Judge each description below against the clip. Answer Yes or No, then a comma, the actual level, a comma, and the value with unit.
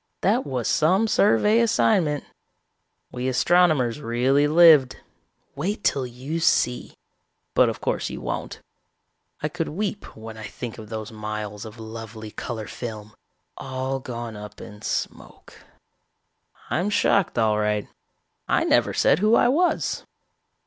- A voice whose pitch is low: Yes, low, 125 Hz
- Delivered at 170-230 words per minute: No, slow, 135 wpm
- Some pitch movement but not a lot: No, wide, 7.6 semitones